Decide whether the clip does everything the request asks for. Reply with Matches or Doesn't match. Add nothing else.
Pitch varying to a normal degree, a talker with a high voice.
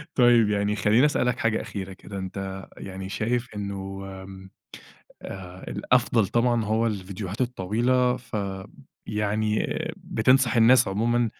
Doesn't match